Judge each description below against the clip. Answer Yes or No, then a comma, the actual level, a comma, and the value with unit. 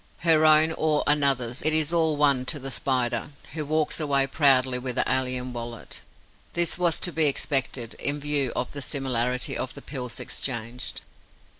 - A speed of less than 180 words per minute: Yes, average, 170 wpm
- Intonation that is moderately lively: Yes, average, 3.4 semitones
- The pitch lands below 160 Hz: Yes, medium, 140 Hz